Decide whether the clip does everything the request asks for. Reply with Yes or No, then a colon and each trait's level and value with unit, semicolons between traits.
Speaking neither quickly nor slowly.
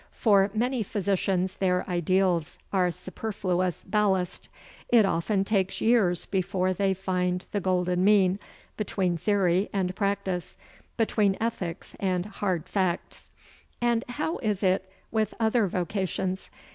No: slow, 120 wpm